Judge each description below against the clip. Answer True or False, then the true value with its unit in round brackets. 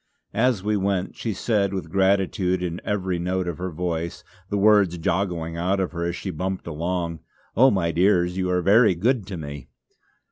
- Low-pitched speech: True (90 Hz)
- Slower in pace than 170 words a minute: False (185 wpm)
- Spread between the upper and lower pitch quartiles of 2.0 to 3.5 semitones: True (2.4 semitones)